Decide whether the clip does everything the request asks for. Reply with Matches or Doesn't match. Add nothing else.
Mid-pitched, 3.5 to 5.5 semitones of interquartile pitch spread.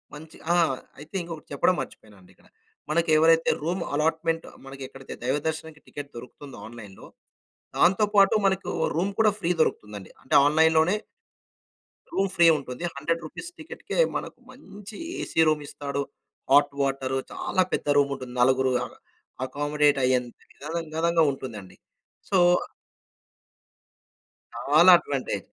Matches